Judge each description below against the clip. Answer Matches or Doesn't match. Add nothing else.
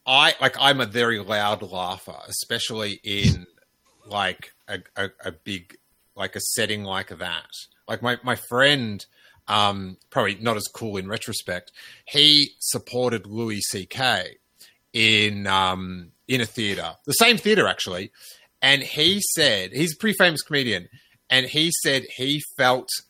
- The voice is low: Matches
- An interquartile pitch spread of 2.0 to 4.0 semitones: Doesn't match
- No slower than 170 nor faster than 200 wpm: Doesn't match